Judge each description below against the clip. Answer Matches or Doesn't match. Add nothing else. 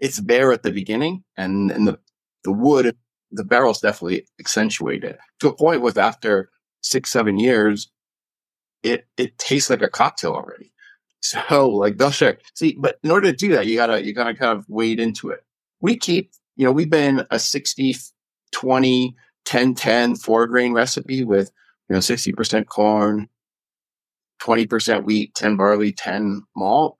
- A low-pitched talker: Matches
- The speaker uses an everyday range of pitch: Matches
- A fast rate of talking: Doesn't match